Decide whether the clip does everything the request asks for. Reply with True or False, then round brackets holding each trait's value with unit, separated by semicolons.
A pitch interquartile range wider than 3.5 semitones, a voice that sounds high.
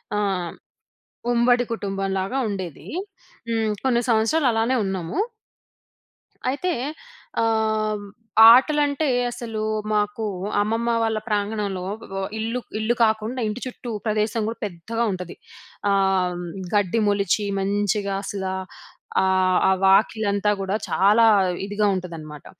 False (2.8 semitones; 210 Hz)